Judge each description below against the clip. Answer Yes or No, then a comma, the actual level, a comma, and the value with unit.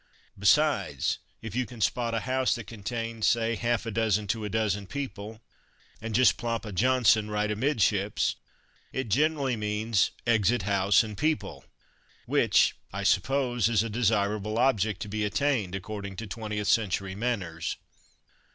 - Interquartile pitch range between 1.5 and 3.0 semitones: Yes, average, 2.7 semitones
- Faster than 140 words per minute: Yes, average, 150 wpm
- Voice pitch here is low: Yes, low, 110 Hz